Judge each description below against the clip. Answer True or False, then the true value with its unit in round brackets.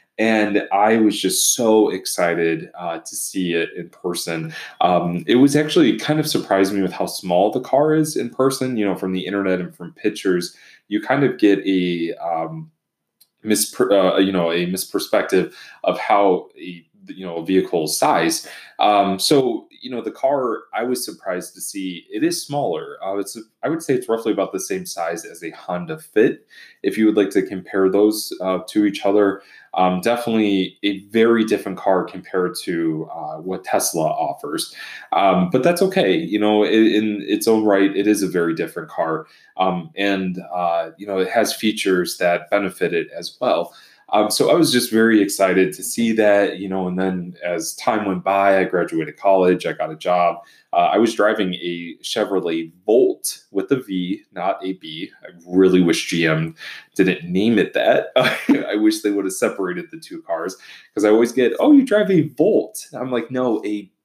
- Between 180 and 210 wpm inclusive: True (195 wpm)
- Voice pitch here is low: True (100 Hz)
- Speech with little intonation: False (4.3 semitones)